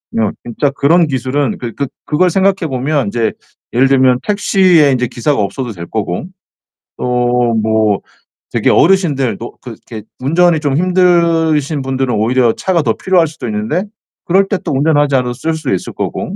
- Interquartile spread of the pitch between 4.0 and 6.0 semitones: Yes, wide, 5.5 semitones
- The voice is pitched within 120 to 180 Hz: Yes, medium, 140 Hz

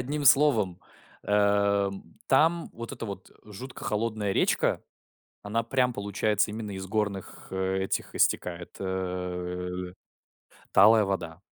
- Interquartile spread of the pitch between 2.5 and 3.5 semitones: Yes, average, 2.9 semitones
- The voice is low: Yes, low, 100 Hz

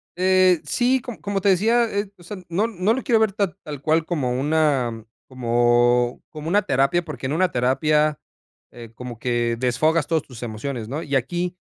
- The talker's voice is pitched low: No, medium, 155 Hz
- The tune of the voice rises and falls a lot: Yes, wide, 6.9 semitones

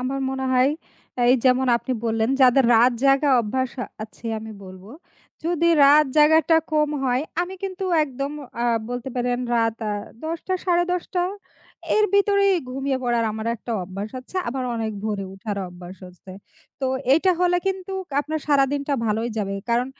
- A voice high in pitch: Yes, very high, 260 Hz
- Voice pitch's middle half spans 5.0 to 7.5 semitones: Yes, wide, 5.4 semitones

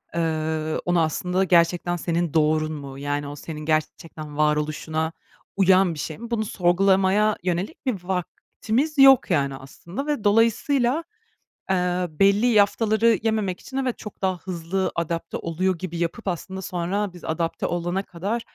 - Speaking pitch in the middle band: Yes, medium, 180 Hz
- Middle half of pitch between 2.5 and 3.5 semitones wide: No, average, 4.3 semitones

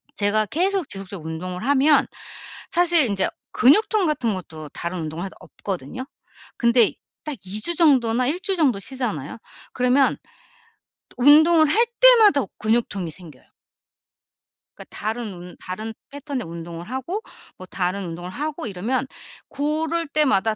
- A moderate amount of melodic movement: No, wide, 8.4 semitones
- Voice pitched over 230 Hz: Yes, high, 240 Hz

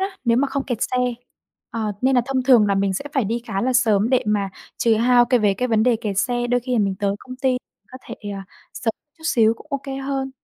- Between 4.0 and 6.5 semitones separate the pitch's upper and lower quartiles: No, average, 3.4 semitones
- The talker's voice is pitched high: Yes, high, 240 Hz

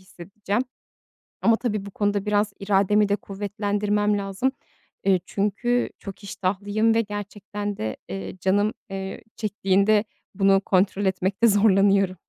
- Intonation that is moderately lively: No, narrow, 1.3 semitones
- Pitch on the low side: No, high, 205 Hz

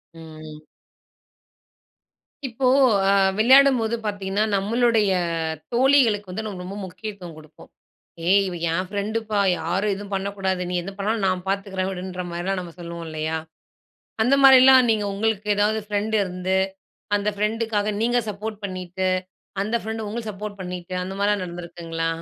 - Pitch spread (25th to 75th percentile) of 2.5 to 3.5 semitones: Yes, average, 3.2 semitones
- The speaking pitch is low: No, high, 200 Hz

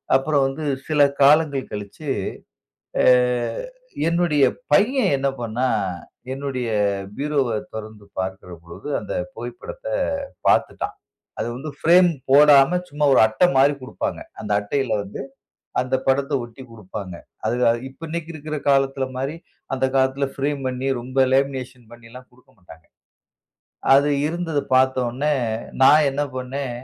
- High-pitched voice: No, low, 135 Hz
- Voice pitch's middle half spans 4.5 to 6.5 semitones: No, average, 3.0 semitones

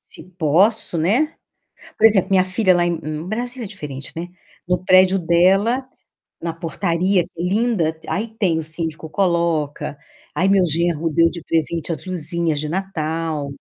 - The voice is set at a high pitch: No, medium, 170 Hz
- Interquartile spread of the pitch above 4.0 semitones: No, average, 3.0 semitones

